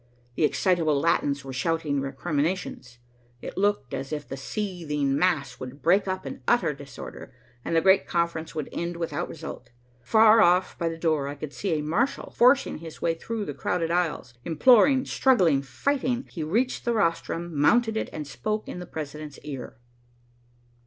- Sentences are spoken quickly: No, average, 170 wpm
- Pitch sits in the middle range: Yes, medium, 165 Hz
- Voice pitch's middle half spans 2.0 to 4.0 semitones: No, average, 4.9 semitones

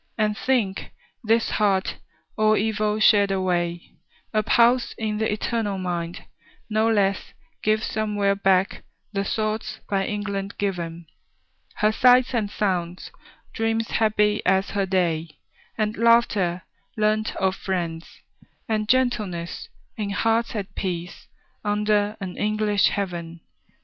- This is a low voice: No, high, 205 Hz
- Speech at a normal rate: No, slow, 120 wpm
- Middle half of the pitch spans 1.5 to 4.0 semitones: Yes, narrow, 2.4 semitones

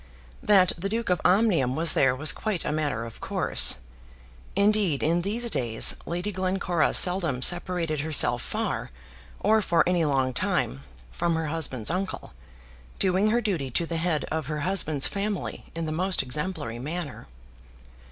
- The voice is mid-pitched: Yes, medium, 170 Hz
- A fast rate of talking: No, average, 155 wpm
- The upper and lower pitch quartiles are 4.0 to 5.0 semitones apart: Yes, average, 4.3 semitones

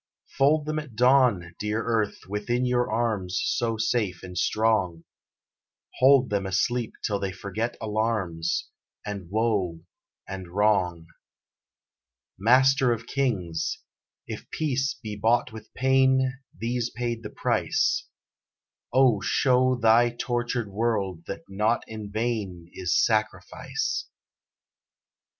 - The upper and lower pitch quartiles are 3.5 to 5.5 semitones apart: Yes, average, 3.8 semitones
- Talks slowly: Yes, slow, 115 wpm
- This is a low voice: Yes, low, 110 Hz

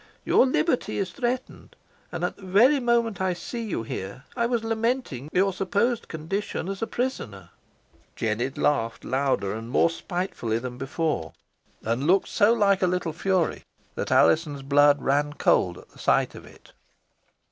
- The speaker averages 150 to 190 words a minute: Yes, average, 160 wpm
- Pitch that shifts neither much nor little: No, wide, 8.7 semitones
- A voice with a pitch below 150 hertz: No, medium, 175 Hz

